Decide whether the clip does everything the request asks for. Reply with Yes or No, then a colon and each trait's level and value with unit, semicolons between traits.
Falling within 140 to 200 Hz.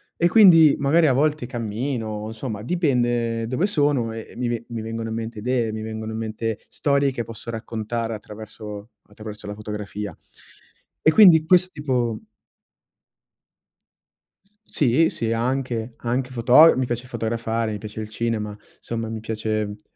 No: low, 115 Hz